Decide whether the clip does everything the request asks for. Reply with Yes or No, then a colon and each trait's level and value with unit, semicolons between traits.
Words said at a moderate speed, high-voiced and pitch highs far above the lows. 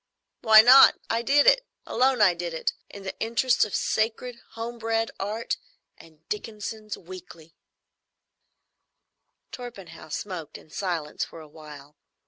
No: slow, 130 wpm; high, 210 Hz; wide, 5.8 semitones